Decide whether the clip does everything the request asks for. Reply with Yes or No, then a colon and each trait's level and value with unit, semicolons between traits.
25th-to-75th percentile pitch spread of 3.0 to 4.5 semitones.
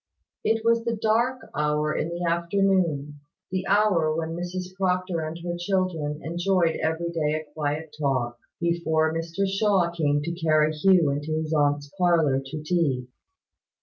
Yes: average, 3.3 semitones